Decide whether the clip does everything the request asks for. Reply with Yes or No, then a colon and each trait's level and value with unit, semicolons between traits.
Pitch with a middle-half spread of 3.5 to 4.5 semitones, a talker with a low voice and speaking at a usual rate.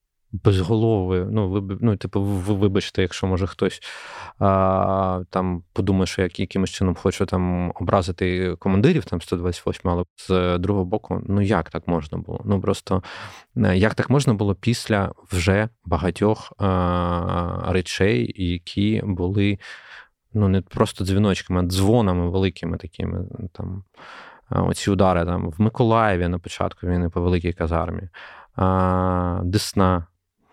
No: narrow, 2.4 semitones; very low, 95 Hz; average, 135 wpm